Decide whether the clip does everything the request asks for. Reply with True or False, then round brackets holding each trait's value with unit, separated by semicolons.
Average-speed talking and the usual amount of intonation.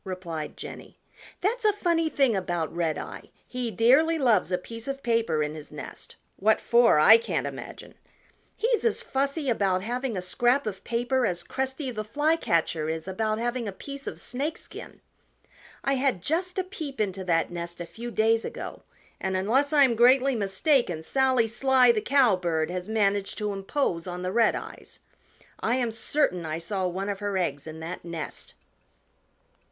False (170 wpm; 6.6 semitones)